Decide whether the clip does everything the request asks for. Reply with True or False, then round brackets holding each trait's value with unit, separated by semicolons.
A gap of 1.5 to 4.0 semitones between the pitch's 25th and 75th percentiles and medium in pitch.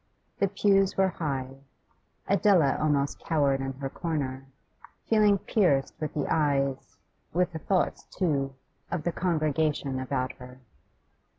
False (5.0 semitones; 150 Hz)